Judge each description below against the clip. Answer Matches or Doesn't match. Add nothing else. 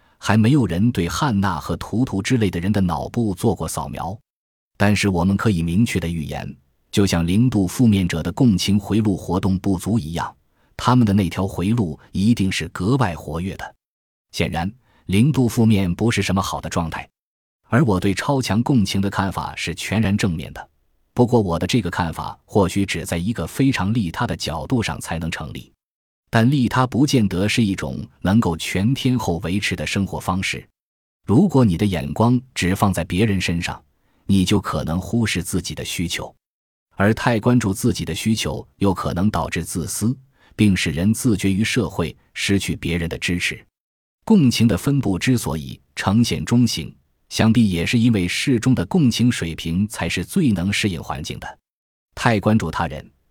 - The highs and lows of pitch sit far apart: Doesn't match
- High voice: Doesn't match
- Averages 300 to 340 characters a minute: Doesn't match